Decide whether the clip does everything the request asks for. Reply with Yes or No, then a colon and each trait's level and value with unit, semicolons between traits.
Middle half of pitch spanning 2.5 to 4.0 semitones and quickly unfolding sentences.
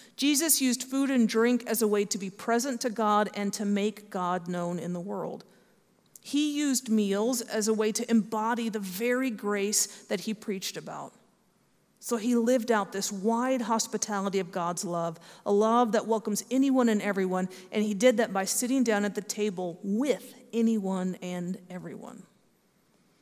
No: average, 3.1 semitones; average, 175 wpm